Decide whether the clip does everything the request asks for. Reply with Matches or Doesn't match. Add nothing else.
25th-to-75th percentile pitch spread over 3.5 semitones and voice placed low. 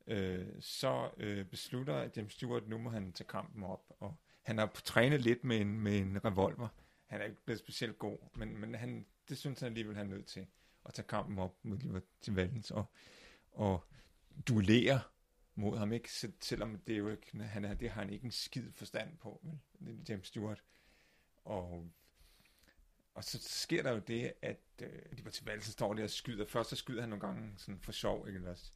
Doesn't match